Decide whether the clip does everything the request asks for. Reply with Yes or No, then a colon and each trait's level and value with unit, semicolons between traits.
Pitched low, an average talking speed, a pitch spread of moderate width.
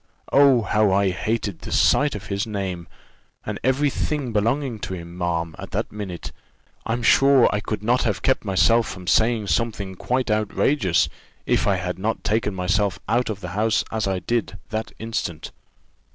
Yes: low, 105 Hz; average, 175 wpm; average, 3.7 semitones